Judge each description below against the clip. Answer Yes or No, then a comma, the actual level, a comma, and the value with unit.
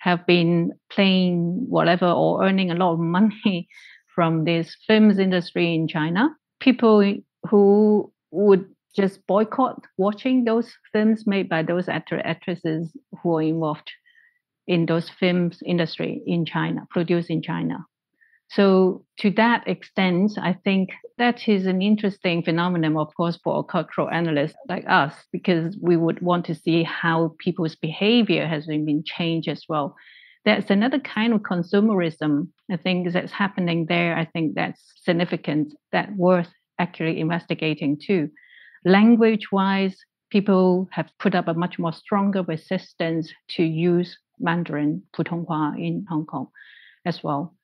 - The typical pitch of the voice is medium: Yes, medium, 180 Hz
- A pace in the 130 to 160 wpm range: Yes, average, 140 wpm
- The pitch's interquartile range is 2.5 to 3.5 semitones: Yes, average, 3.2 semitones